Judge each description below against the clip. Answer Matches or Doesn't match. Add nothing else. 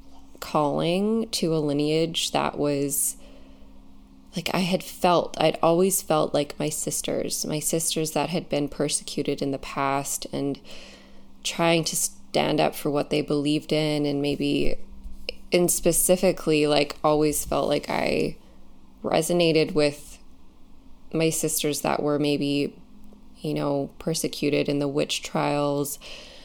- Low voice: Doesn't match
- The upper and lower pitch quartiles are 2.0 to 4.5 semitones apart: Matches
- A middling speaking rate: Doesn't match